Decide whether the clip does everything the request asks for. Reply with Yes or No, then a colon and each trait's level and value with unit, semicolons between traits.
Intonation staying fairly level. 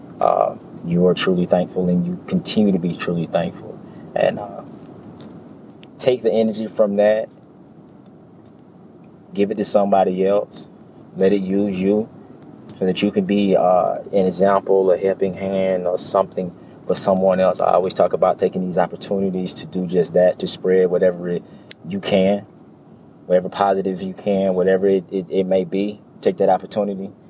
Yes: narrow, 1.6 semitones